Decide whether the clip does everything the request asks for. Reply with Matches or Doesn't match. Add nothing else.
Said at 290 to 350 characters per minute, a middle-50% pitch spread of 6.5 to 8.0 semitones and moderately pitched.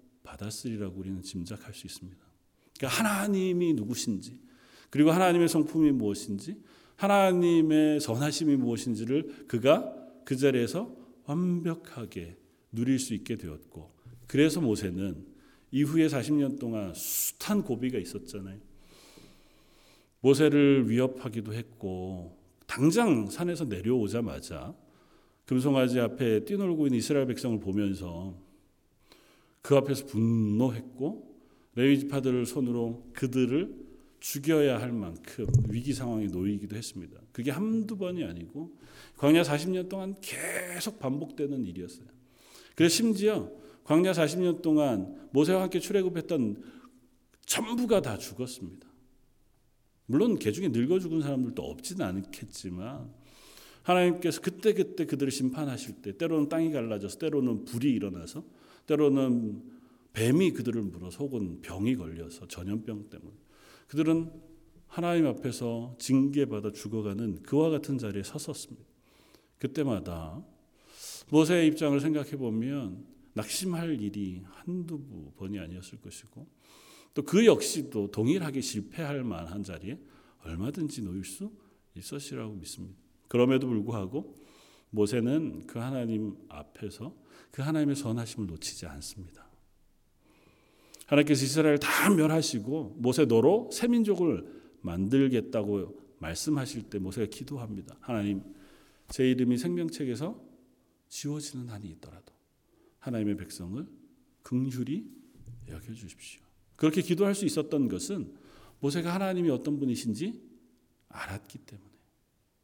Doesn't match